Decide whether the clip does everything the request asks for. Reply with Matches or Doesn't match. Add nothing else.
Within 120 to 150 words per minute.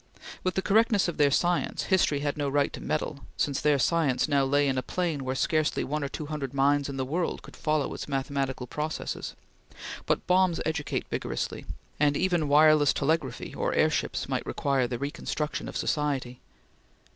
Doesn't match